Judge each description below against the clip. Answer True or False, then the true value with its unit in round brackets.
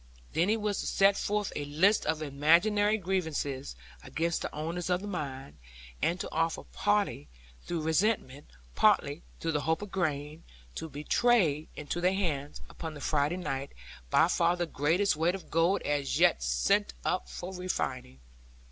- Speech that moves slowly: False (165 wpm)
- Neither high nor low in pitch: True (165 Hz)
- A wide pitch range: False (4.5 semitones)